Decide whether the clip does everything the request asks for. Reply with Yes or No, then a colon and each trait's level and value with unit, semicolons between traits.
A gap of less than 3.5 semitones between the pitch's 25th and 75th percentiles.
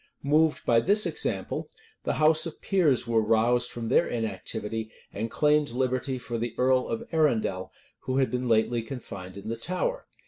No: average, 4.8 semitones